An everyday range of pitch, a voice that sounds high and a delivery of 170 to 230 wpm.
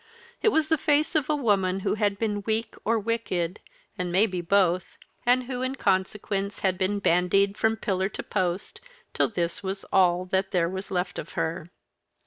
Yes: average, 3.4 semitones; high, 195 Hz; average, 180 wpm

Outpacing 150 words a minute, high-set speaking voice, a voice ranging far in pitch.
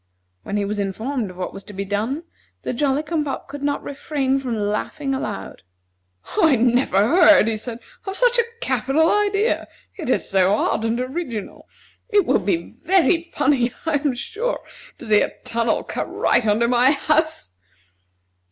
Yes: average, 170 wpm; very high, 260 Hz; wide, 6.4 semitones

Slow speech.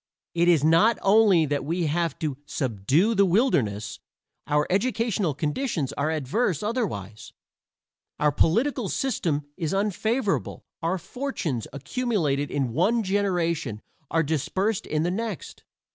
Yes: slow, 130 wpm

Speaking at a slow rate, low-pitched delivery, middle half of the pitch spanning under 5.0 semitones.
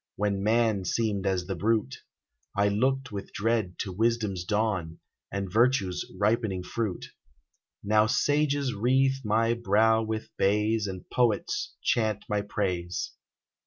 Yes: slow, 125 wpm; low, 105 Hz; average, 2.9 semitones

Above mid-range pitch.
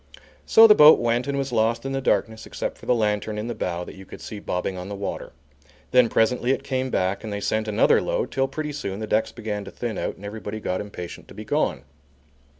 No: low, 110 Hz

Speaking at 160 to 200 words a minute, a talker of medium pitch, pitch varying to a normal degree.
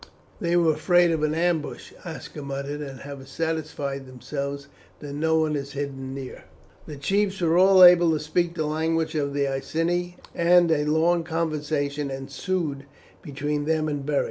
Yes: average, 165 wpm; medium, 155 Hz; average, 3.0 semitones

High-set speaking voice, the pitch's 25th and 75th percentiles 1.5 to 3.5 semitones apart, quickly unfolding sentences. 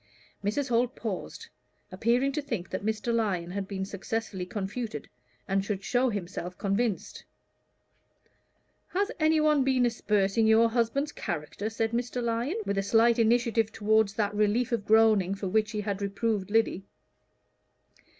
No: high, 220 Hz; average, 3.1 semitones; average, 145 wpm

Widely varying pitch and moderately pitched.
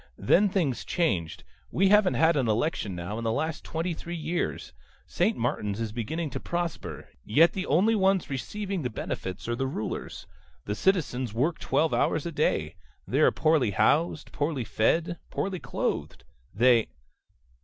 Yes: wide, 7.3 semitones; medium, 150 Hz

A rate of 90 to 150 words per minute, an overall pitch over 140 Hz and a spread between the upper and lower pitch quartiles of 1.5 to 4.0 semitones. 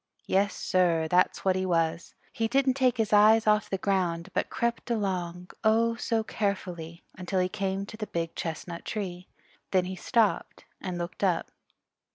No: average, 170 wpm; high, 190 Hz; average, 3.6 semitones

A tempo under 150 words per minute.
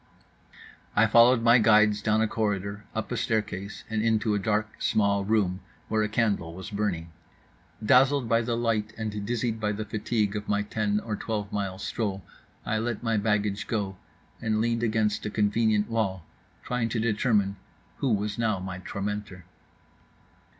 No: average, 165 wpm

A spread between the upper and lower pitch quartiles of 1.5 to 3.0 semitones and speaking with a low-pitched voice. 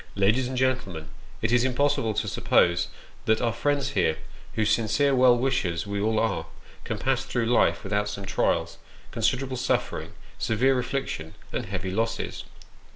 No: average, 4.4 semitones; low, 115 Hz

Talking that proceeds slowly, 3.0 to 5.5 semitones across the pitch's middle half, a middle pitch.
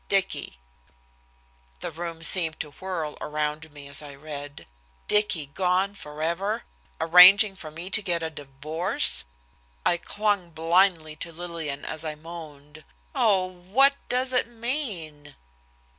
Yes: slow, 130 wpm; average, 4.0 semitones; medium, 170 Hz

